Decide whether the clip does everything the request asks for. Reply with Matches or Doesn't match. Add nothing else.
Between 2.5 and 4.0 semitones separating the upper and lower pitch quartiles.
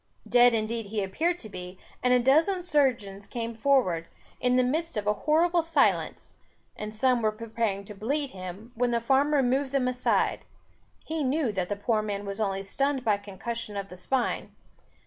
Doesn't match